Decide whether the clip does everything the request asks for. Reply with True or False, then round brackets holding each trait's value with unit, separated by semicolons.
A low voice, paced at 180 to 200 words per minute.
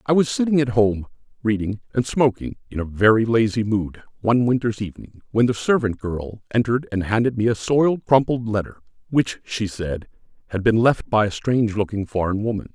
True (115 Hz; 190 wpm)